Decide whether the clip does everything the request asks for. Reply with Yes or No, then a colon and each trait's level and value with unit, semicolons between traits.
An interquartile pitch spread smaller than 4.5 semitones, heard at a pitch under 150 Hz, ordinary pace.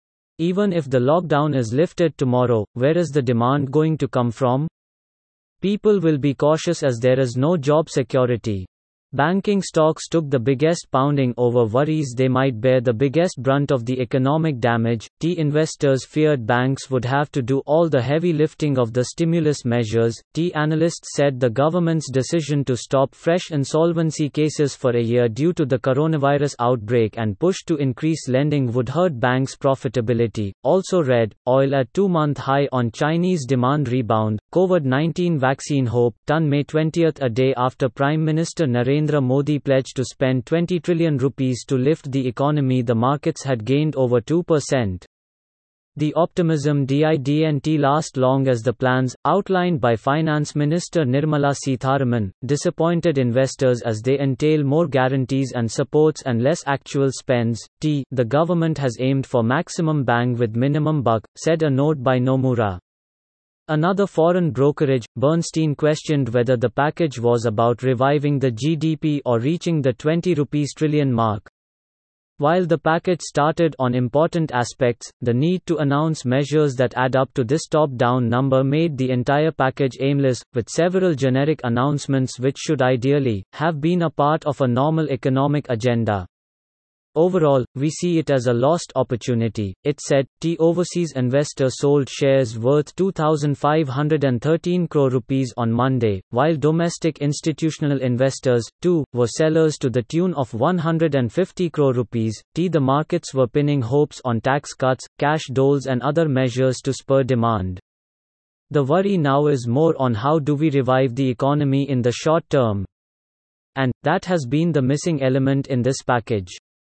Yes: average, 3.6 semitones; medium, 140 Hz; average, 160 wpm